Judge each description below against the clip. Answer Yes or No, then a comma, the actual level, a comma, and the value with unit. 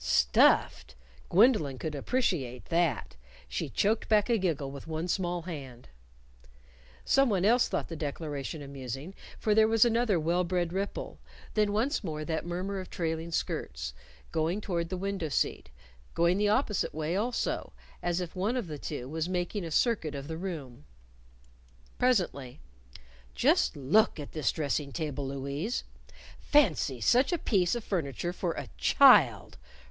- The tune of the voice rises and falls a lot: Yes, wide, 5.9 semitones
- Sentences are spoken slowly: No, average, 150 wpm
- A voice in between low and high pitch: Yes, medium, 170 Hz